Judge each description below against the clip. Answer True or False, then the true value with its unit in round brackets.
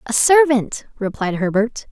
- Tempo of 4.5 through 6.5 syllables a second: False (4.2 syllables/s)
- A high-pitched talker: True (240 Hz)